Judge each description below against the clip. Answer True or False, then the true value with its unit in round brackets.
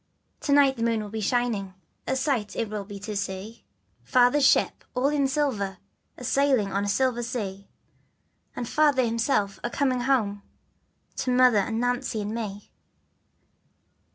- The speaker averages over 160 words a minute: False (155 wpm)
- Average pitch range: True (4.1 semitones)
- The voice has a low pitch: False (235 Hz)